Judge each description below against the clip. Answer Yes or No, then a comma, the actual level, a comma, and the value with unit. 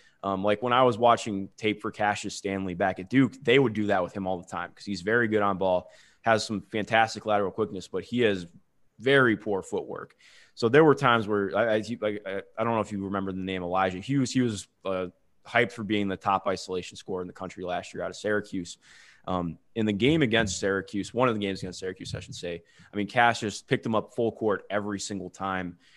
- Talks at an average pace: No, fast, 235 wpm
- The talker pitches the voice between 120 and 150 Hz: No, low, 100 Hz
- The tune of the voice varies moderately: Yes, average, 3.0 semitones